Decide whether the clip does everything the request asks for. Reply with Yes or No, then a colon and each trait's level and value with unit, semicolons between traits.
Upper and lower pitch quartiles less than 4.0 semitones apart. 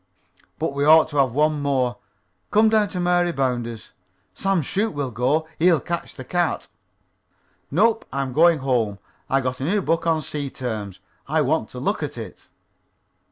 No: average, 5.1 semitones